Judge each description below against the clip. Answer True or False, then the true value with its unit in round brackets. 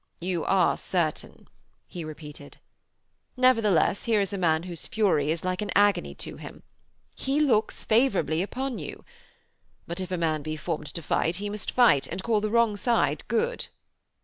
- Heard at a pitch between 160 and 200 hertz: True (190 Hz)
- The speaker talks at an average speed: True (170 wpm)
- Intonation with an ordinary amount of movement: True (5.0 semitones)